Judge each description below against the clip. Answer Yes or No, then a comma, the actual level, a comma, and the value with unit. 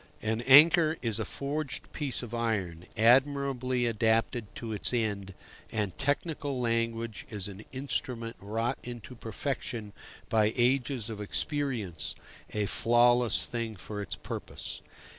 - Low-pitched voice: Yes, low, 115 Hz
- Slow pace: Yes, slow, 125 wpm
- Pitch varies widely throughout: No, average, 3.3 semitones